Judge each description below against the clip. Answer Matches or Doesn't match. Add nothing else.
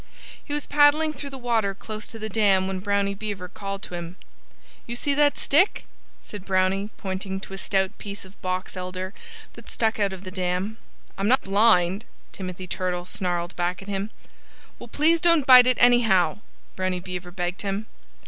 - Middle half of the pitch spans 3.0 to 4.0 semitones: Matches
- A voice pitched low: Doesn't match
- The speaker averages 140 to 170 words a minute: Doesn't match